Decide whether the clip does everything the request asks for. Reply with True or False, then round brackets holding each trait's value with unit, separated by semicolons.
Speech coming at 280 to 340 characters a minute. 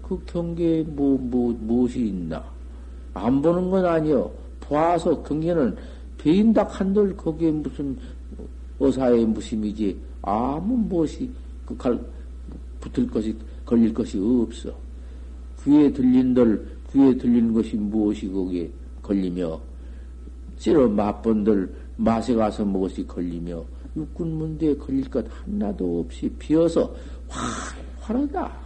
False (235 characters per minute)